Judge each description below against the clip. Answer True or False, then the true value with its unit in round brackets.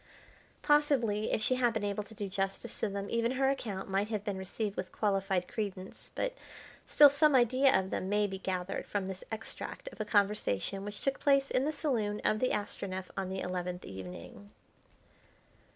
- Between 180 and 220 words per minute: True (185 wpm)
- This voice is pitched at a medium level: False (205 Hz)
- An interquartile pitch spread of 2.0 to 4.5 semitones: True (3.9 semitones)